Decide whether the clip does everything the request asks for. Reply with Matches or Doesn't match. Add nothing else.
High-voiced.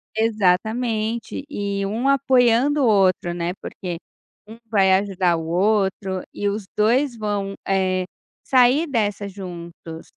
Matches